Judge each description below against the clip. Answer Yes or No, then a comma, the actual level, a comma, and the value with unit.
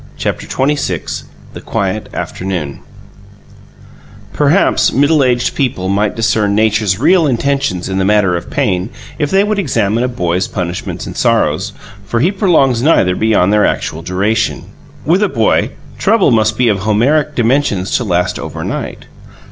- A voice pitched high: No, low, 110 Hz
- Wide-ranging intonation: Yes, wide, 6.4 semitones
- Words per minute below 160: Yes, average, 150 wpm